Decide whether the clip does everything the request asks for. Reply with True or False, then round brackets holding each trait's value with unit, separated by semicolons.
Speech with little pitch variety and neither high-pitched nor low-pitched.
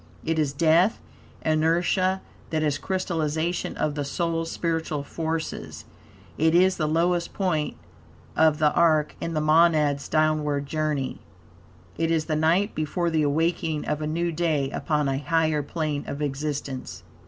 True (1.9 semitones; 155 Hz)